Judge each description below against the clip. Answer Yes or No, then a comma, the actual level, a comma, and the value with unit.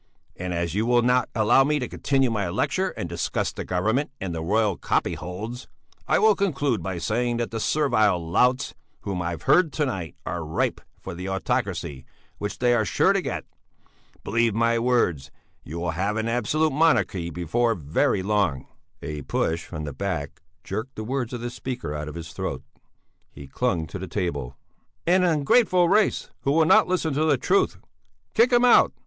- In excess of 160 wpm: Yes, average, 190 wpm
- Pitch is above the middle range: No, low, 110 Hz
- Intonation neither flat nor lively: No, wide, 7.1 semitones